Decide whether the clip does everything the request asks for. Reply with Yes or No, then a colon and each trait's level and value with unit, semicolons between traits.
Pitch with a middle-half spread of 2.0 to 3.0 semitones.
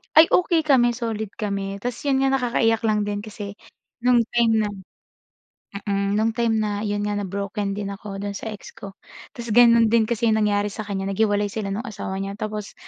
Yes: narrow, 2.4 semitones